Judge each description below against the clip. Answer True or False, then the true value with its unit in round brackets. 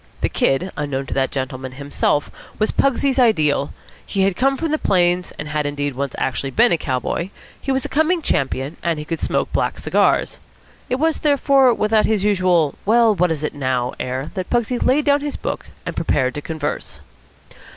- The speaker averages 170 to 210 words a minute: True (190 wpm)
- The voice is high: False (175 Hz)